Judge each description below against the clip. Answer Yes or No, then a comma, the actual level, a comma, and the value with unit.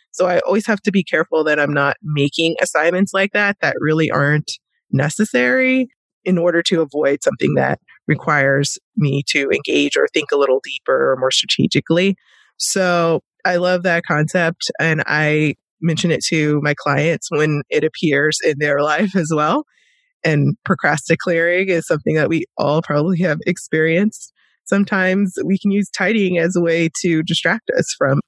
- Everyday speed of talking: Yes, average, 165 wpm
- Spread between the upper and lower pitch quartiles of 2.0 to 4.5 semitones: Yes, average, 3.7 semitones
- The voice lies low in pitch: No, medium, 165 Hz